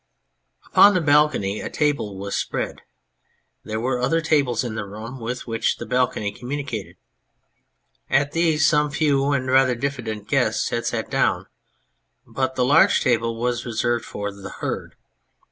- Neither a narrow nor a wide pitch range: Yes, average, 4.3 semitones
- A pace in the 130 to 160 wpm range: Yes, average, 155 wpm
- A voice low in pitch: Yes, low, 125 Hz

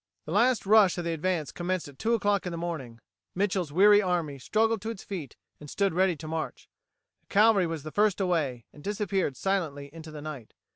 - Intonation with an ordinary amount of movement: Yes, average, 4.7 semitones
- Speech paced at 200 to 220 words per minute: Yes, fast, 205 wpm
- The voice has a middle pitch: Yes, medium, 180 Hz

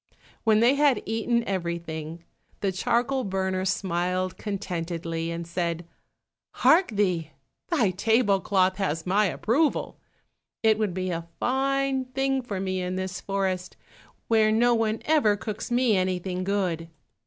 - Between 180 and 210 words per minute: No, slow, 135 wpm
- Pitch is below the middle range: No, high, 195 Hz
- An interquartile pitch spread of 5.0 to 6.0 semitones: No, average, 4.1 semitones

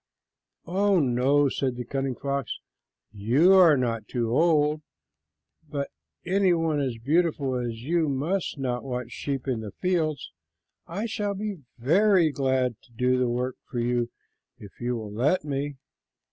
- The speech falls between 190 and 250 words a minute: No, average, 145 wpm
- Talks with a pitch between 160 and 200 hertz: No, low, 135 Hz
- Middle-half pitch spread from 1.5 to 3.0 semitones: No, average, 5.1 semitones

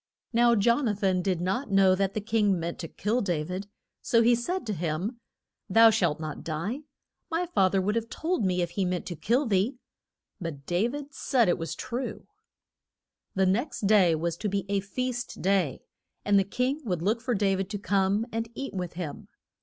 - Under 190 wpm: No, fast, 205 wpm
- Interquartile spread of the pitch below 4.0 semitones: No, average, 4.3 semitones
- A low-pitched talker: No, high, 200 Hz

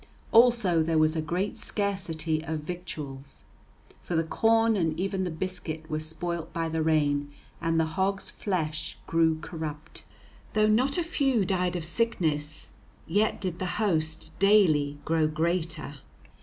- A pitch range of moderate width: Yes, average, 3.7 semitones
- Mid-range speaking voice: Yes, medium, 165 Hz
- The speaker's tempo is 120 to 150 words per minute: Yes, average, 145 wpm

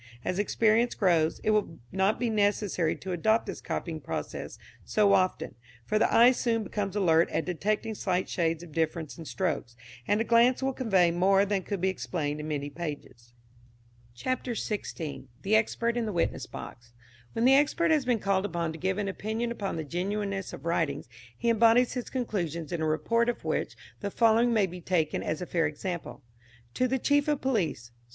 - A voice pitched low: No, high, 195 Hz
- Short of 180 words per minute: No, average, 190 wpm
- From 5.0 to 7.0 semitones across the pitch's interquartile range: Yes, wide, 5.4 semitones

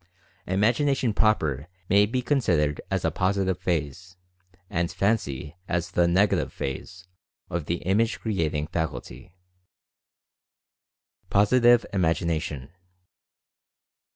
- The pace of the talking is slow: Yes, slow, 100 wpm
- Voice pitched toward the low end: Yes, very low, 90 Hz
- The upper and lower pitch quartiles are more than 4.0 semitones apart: Yes, average, 4.4 semitones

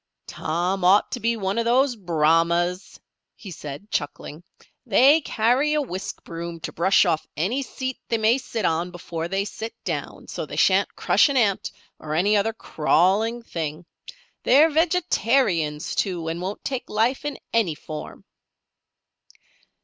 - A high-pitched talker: Yes, high, 200 Hz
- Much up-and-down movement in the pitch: Yes, wide, 6.1 semitones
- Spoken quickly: No, average, 150 wpm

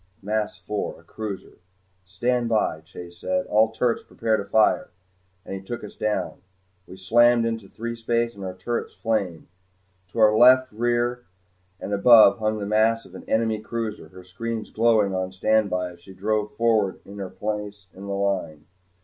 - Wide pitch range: No, average, 2.9 semitones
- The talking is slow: No, average, 170 wpm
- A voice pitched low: Yes, low, 110 Hz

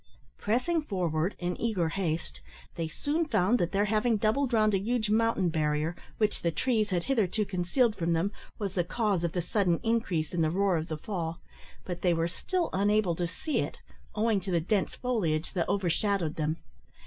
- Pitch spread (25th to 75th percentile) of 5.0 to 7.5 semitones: No, average, 4.4 semitones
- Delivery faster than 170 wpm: Yes, average, 190 wpm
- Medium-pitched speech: No, high, 195 Hz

